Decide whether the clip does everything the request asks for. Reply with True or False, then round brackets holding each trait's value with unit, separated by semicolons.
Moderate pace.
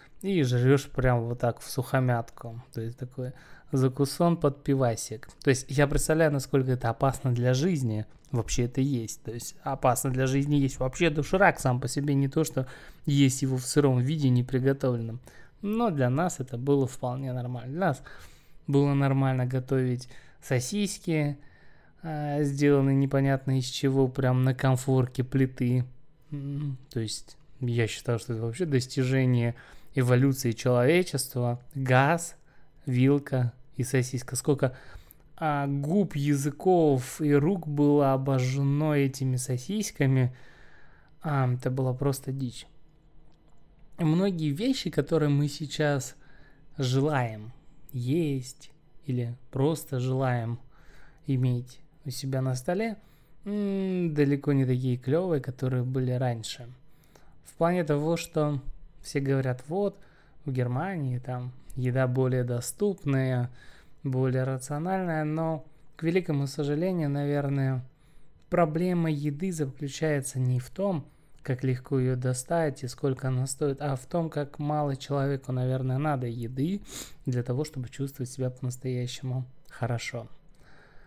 True (125 wpm)